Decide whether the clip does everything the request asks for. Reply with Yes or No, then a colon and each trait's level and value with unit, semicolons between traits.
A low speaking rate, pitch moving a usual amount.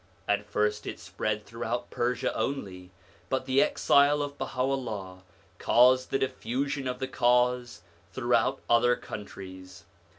Yes: slow, 130 wpm; average, 3.9 semitones